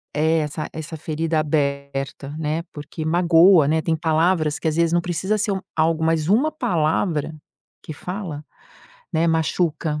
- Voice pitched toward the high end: No, medium, 160 Hz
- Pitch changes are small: Yes, narrow, 1.9 semitones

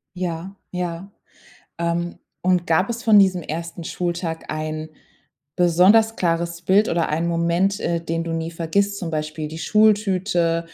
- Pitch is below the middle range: No, medium, 170 Hz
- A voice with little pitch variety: Yes, narrow, 2.3 semitones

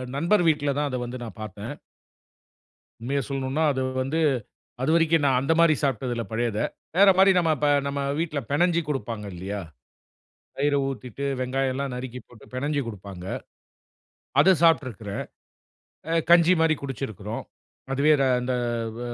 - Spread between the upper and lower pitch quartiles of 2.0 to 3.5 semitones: No, average, 4.4 semitones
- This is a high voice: No, low, 135 Hz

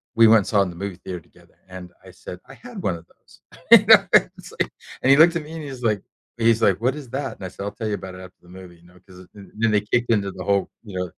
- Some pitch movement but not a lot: Yes, average, 4.3 semitones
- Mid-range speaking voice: No, low, 100 Hz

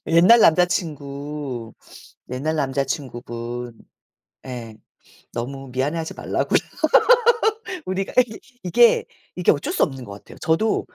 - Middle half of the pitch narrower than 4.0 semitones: No, average, 5.3 semitones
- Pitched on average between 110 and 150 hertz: Yes, medium, 140 Hz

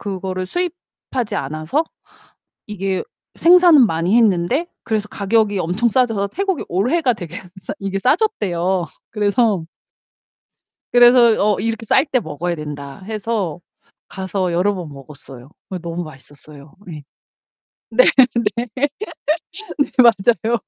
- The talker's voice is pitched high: Yes, high, 200 Hz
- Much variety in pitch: Yes, wide, 5.7 semitones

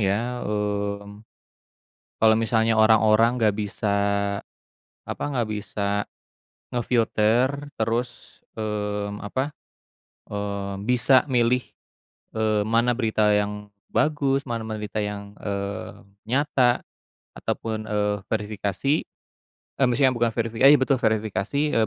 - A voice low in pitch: Yes, low, 110 Hz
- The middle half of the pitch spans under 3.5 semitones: Yes, average, 2.9 semitones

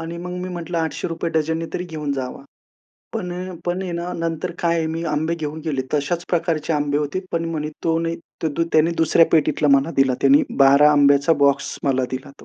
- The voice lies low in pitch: No, medium, 160 Hz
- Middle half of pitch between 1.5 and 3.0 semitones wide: Yes, average, 2.7 semitones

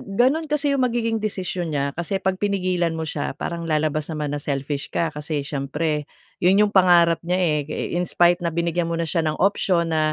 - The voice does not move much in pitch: No, average, 3.4 semitones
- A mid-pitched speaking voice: Yes, medium, 170 Hz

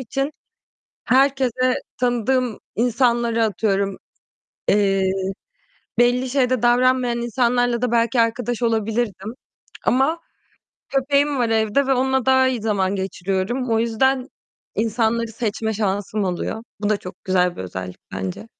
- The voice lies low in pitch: No, high, 235 Hz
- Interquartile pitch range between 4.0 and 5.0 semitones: No, average, 3.4 semitones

